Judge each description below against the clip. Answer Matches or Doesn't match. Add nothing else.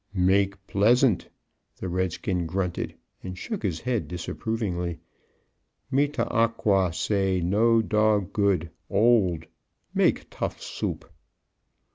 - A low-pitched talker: Matches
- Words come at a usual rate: Doesn't match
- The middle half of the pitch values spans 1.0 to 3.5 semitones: Doesn't match